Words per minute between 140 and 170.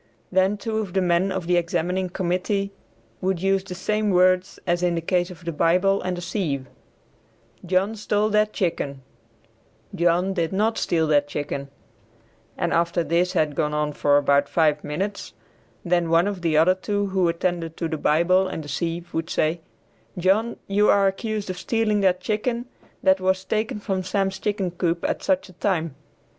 No: average, 180 wpm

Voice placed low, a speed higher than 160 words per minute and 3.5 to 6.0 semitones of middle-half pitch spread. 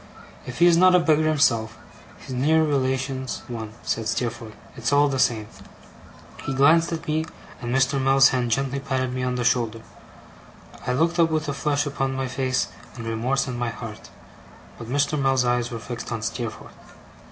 No: low, 130 Hz; average, 185 wpm; average, 3.0 semitones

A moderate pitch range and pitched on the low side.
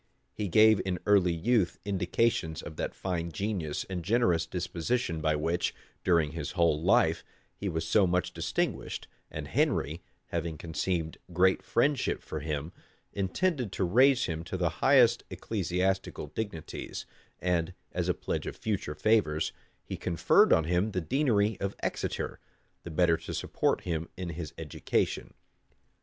Yes: average, 3.9 semitones; very low, 90 Hz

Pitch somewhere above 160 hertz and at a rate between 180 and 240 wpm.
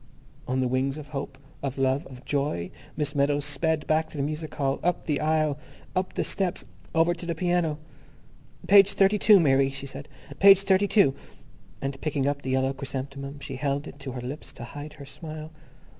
No: medium, 145 Hz; average, 195 wpm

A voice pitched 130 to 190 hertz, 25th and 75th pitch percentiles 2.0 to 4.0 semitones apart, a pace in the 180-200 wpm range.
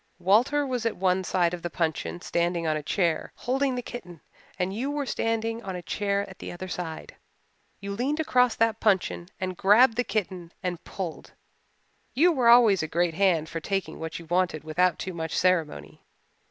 No: medium, 185 Hz; average, 4.9 semitones; average, 190 wpm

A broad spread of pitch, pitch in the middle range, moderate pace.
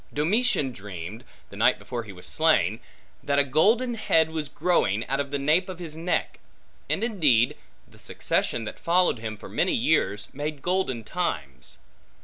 Yes: wide, 7.8 semitones; medium, 145 Hz; average, 165 wpm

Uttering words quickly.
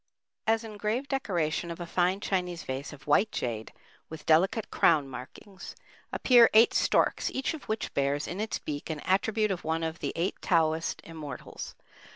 No: average, 170 wpm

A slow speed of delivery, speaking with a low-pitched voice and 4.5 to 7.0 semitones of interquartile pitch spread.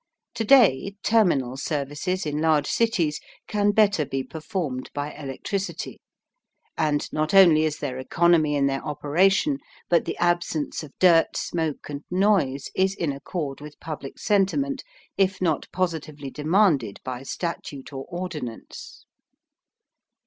No: slow, 130 wpm; medium, 160 Hz; average, 4.8 semitones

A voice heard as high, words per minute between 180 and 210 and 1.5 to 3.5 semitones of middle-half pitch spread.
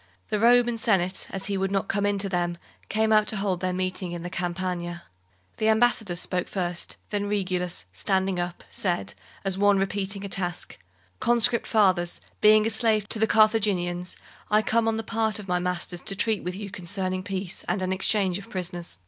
Yes: high, 195 Hz; average, 190 wpm; average, 2.9 semitones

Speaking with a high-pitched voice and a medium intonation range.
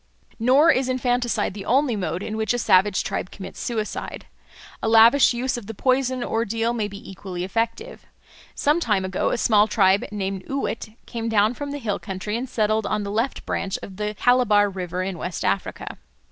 Yes: high, 220 Hz; average, 3.6 semitones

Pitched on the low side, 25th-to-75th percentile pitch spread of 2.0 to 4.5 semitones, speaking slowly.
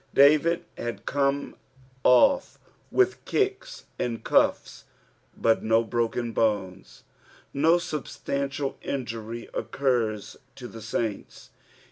Yes: low, 125 Hz; average, 4.2 semitones; slow, 95 wpm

